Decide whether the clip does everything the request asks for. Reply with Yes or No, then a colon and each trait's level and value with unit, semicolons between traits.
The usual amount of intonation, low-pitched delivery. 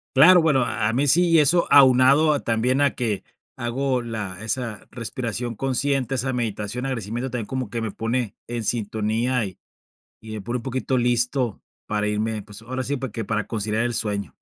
Yes: average, 3.2 semitones; low, 120 Hz